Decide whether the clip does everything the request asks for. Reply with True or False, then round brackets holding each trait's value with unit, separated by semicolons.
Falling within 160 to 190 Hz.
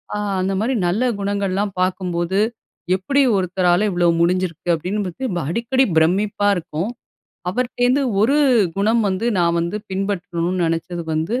True (185 Hz)